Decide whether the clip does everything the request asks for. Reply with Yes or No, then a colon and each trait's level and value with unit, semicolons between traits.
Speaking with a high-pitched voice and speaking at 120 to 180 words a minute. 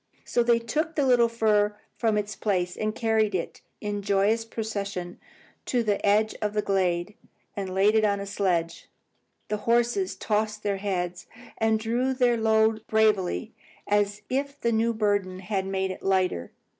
Yes: high, 210 Hz; average, 165 wpm